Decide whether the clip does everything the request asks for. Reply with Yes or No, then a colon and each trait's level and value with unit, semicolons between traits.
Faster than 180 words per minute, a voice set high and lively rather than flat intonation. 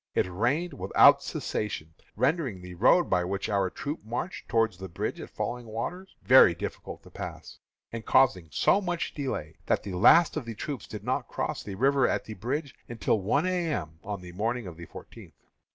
No: average, 190 wpm; low, 115 Hz; wide, 7.2 semitones